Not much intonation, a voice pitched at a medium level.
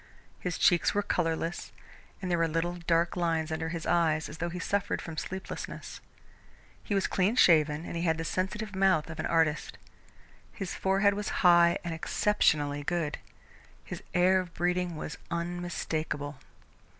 Yes: narrow, 2.2 semitones; medium, 170 Hz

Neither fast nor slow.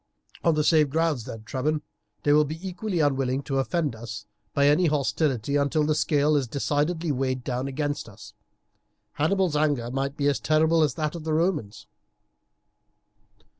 Yes: average, 165 wpm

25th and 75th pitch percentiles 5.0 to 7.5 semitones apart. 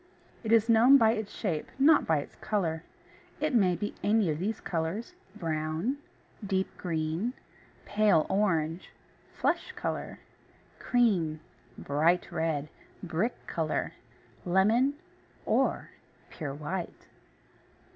Yes: wide, 5.5 semitones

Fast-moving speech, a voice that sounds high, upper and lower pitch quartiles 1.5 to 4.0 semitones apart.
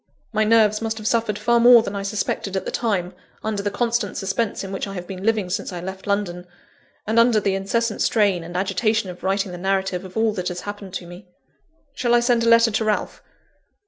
Yes: fast, 225 wpm; high, 205 Hz; average, 2.9 semitones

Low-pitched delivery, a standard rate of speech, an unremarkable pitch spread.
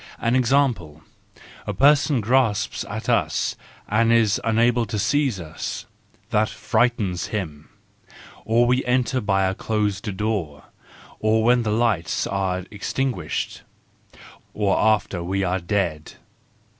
No: low, 110 Hz; slow, 120 wpm; average, 3.9 semitones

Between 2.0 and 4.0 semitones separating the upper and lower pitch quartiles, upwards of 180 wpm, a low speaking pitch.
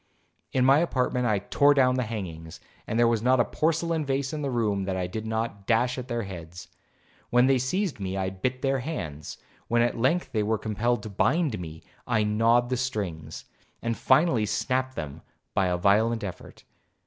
No: average, 4.7 semitones; average, 195 wpm; low, 115 Hz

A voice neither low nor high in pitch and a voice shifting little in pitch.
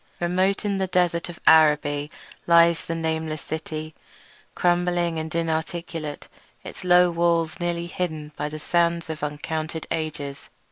Yes: medium, 165 Hz; narrow, 1.8 semitones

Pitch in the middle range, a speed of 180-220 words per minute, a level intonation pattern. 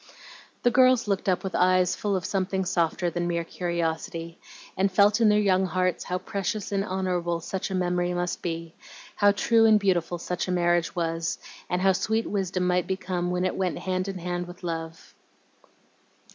Yes: medium, 180 Hz; average, 185 wpm; narrow, 1.9 semitones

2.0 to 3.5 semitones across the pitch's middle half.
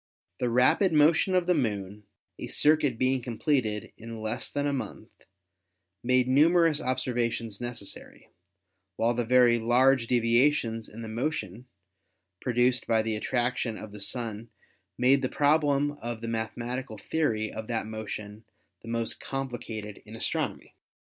Yes: average, 3.0 semitones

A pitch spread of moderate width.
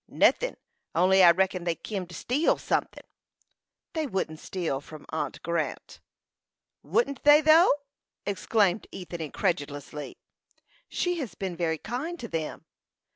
No: wide, 7.8 semitones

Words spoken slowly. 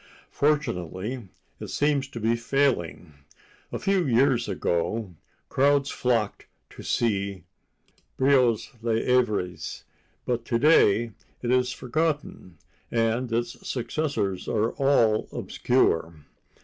Yes: slow, 105 wpm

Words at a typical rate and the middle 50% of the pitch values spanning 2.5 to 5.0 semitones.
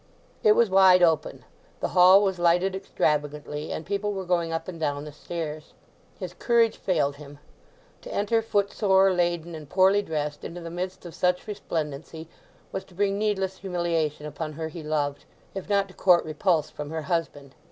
Yes: average, 175 wpm; average, 3.8 semitones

